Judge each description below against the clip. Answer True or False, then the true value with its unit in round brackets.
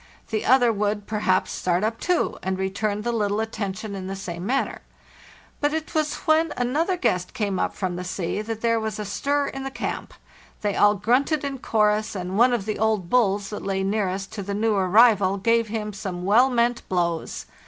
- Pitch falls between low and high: False (210 Hz)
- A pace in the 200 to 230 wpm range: True (205 wpm)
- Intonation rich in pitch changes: False (3.5 semitones)